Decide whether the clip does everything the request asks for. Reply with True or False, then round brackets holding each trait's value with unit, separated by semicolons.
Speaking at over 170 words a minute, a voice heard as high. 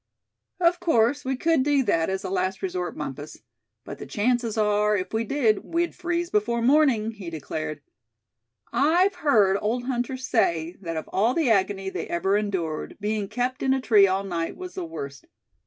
True (180 wpm; 220 Hz)